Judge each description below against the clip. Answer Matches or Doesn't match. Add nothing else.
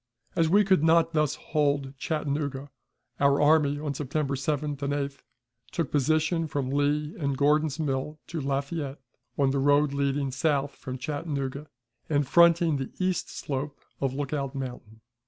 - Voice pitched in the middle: Matches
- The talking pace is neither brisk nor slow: Matches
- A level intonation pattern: Matches